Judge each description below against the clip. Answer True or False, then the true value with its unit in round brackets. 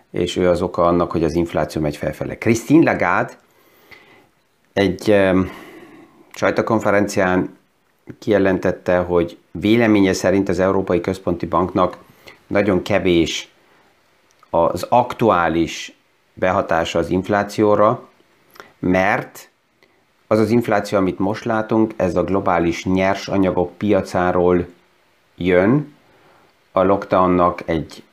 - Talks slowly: True (100 wpm)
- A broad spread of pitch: False (2.6 semitones)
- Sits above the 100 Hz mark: False (95 Hz)